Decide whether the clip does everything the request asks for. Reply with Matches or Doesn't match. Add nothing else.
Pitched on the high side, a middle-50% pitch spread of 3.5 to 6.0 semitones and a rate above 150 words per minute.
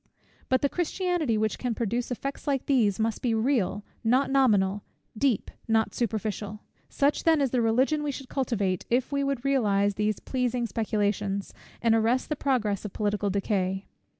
Matches